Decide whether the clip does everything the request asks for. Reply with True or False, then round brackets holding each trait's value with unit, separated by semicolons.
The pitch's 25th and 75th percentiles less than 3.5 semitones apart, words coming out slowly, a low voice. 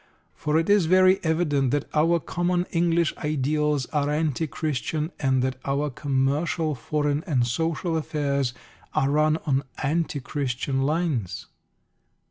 False (3.0 semitones; 130 wpm; 150 Hz)